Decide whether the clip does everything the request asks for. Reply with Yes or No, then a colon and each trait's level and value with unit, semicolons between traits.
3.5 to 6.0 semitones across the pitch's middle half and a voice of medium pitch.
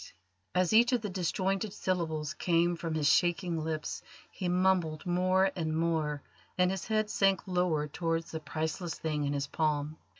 No: average, 3.0 semitones; medium, 170 Hz